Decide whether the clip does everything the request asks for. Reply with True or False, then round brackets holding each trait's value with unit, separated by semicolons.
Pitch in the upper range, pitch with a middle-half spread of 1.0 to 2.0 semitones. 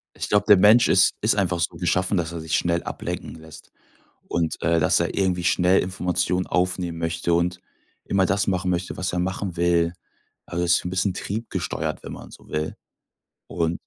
False (90 Hz; 1.7 semitones)